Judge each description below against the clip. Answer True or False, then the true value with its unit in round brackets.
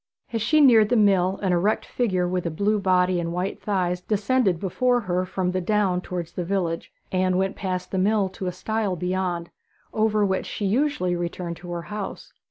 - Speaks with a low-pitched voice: False (185 Hz)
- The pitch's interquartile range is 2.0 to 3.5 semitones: True (2.8 semitones)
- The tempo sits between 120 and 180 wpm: False (195 wpm)